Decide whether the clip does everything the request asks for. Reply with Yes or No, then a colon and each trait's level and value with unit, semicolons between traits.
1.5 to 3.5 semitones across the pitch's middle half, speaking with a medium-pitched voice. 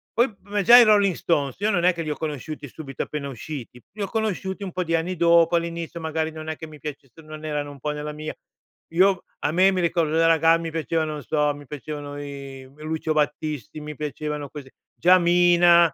Yes: narrow, 2.6 semitones; medium, 160 Hz